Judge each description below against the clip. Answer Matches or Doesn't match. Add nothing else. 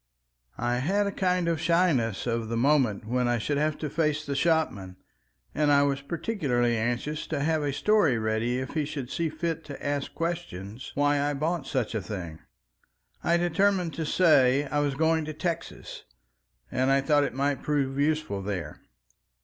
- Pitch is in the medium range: Matches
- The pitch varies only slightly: Doesn't match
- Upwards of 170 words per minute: Matches